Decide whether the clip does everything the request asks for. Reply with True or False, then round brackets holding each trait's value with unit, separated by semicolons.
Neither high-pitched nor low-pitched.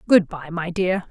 True (175 Hz)